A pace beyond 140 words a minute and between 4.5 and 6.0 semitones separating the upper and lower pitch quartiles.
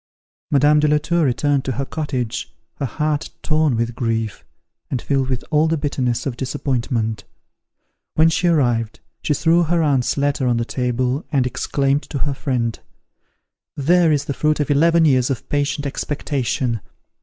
No: average, 165 wpm; average, 3.3 semitones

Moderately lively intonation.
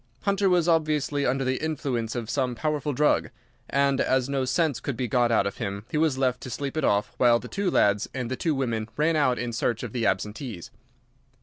Yes: average, 4.2 semitones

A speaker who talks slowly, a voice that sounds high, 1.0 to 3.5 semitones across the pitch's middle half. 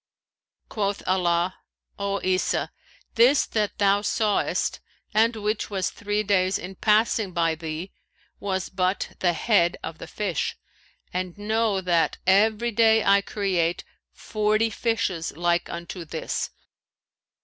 Yes: slow, 125 wpm; high, 195 Hz; average, 3.1 semitones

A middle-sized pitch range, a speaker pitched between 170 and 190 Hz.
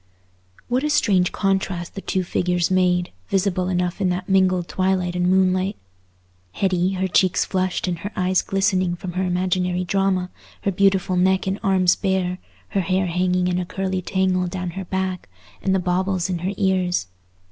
No: narrow, 1.0 semitones; medium, 185 Hz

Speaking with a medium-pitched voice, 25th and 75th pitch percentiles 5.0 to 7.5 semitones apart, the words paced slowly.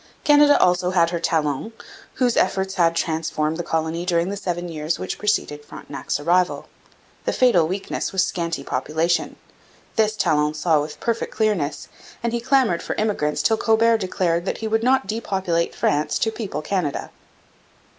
No: medium, 175 Hz; average, 5.3 semitones; average, 165 wpm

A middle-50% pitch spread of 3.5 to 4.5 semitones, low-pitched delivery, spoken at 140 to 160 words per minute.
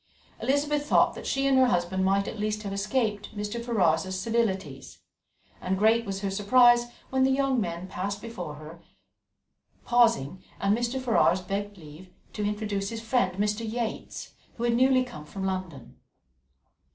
No: average, 4.1 semitones; high, 210 Hz; average, 155 wpm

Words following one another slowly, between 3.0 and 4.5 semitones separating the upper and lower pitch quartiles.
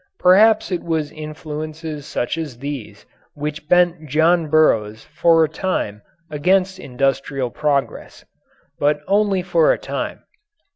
Yes: slow, 125 wpm; average, 3.6 semitones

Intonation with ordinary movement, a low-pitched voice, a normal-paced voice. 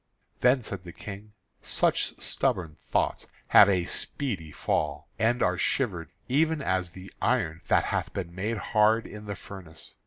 Yes: average, 4.4 semitones; low, 100 Hz; average, 155 wpm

